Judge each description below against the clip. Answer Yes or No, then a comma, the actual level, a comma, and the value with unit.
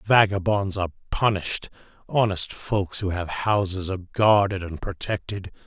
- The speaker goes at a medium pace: No, slow, 125 wpm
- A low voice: Yes, very low, 95 Hz